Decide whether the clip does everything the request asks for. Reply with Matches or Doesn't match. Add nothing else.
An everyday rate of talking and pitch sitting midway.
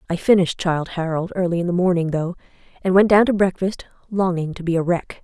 Doesn't match